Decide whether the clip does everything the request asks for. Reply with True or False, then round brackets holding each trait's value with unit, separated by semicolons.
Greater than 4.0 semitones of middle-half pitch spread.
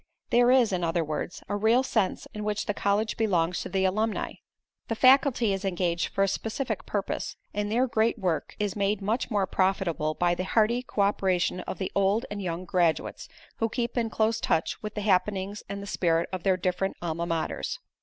False (3.2 semitones)